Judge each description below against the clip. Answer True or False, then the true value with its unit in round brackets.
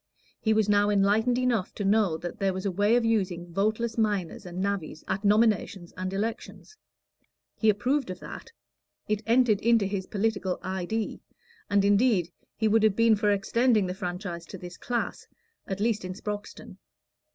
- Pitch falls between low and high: False (205 Hz)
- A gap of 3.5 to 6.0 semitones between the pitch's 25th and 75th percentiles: False (2.8 semitones)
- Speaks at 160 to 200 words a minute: True (170 wpm)